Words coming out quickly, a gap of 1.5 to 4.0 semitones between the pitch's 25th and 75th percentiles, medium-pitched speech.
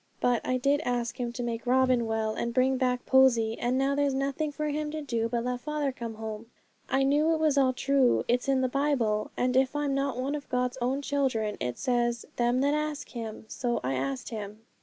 No: fast, 225 wpm; average, 2.8 semitones; very high, 255 Hz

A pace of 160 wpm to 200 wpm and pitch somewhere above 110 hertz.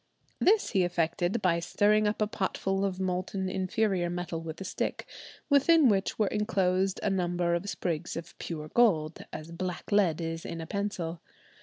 Yes: average, 170 wpm; medium, 185 Hz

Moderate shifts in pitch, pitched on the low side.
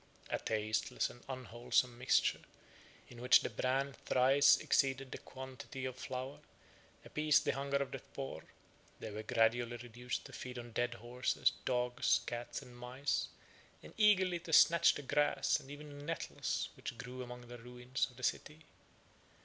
No: narrow, 2.1 semitones; low, 125 Hz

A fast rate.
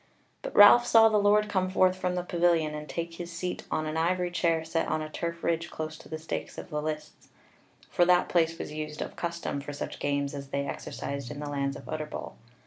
Yes: fast, 225 wpm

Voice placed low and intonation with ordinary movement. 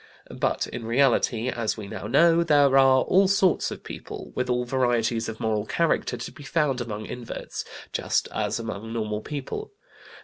Yes: low, 125 Hz; average, 4.2 semitones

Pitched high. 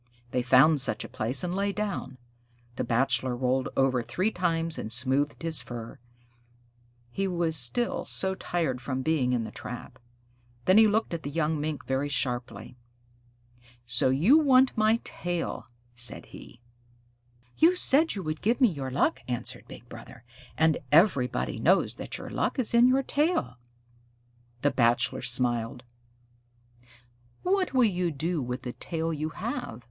No: medium, 150 Hz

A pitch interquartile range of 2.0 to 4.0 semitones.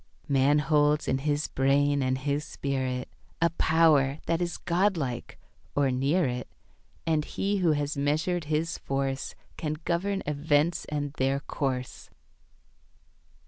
Yes: average, 3.0 semitones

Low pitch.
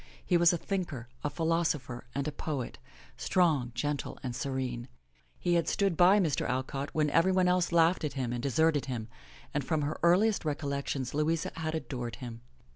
No: medium, 150 Hz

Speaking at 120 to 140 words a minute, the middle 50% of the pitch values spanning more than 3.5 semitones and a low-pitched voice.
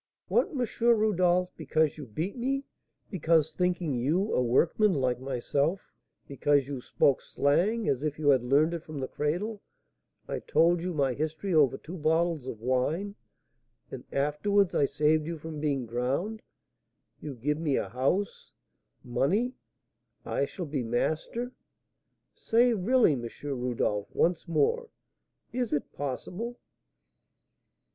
No: slow, 135 wpm; wide, 5.6 semitones; medium, 155 Hz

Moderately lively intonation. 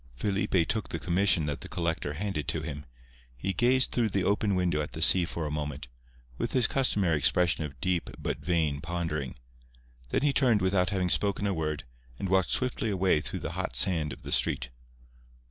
Yes: average, 4.7 semitones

